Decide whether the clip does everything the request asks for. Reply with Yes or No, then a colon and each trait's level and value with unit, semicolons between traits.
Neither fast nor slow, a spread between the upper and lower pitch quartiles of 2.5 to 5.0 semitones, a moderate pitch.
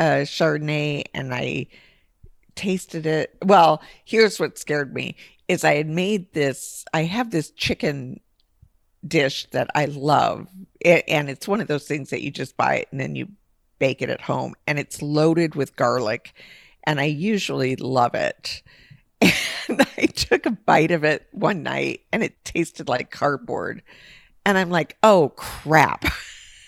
Yes: average, 160 wpm; average, 3.9 semitones; medium, 150 Hz